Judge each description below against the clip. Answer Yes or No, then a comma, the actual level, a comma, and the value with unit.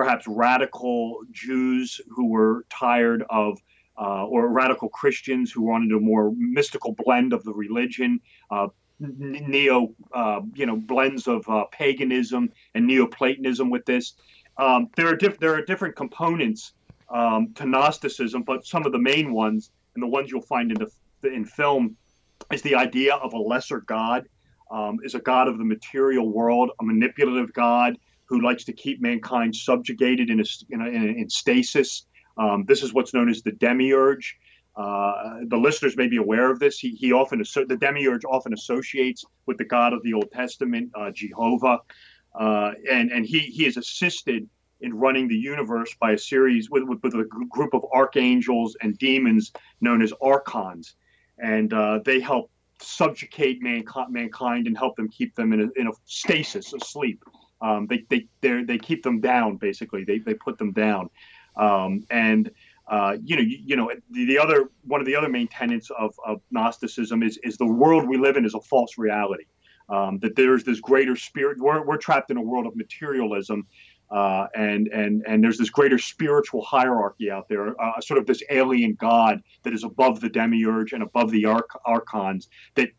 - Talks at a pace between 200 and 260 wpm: No, average, 180 wpm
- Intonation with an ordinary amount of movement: Yes, average, 4.4 semitones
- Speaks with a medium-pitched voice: No, low, 125 Hz